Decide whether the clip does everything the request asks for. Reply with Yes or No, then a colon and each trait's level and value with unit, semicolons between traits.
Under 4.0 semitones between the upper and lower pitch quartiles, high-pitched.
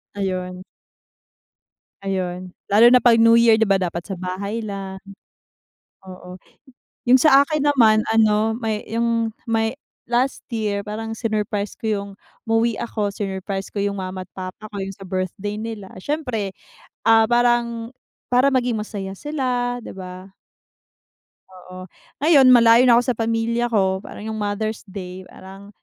Yes: average, 3.3 semitones; high, 215 Hz